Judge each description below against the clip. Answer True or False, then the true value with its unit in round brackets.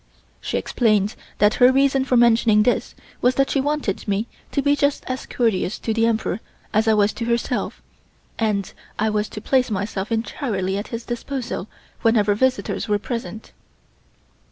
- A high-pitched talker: True (225 Hz)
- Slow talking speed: False (165 wpm)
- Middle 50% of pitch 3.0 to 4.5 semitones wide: True (3.3 semitones)